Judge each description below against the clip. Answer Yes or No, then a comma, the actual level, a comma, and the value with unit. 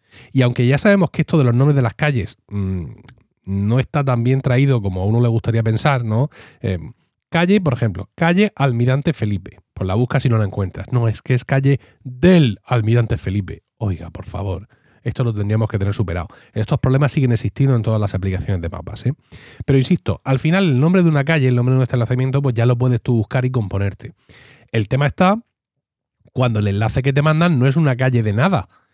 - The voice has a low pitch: Yes, low, 125 Hz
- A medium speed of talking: No, fast, 220 wpm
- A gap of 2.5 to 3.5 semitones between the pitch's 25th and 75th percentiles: No, average, 4.3 semitones